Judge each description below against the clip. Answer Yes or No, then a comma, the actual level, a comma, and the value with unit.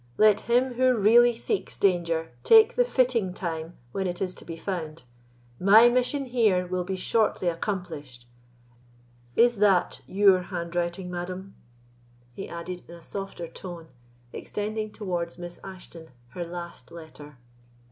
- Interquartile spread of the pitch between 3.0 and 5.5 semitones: Yes, average, 4.0 semitones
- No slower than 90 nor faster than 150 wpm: Yes, slow, 135 wpm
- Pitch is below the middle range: No, medium, 185 Hz